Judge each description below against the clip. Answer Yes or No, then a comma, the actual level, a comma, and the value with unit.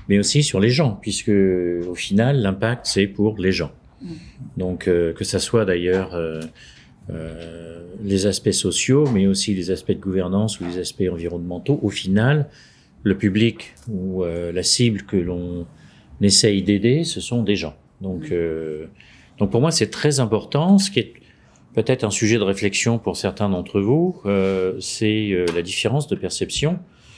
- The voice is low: Yes, low, 100 Hz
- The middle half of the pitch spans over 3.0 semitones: Yes, average, 4.1 semitones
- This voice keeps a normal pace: Yes, average, 170 wpm